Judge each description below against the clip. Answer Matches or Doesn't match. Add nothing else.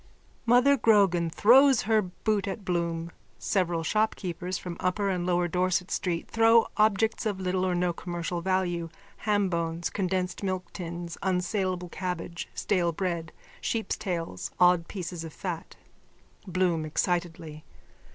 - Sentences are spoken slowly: Matches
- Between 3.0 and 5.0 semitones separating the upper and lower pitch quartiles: Doesn't match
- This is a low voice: Doesn't match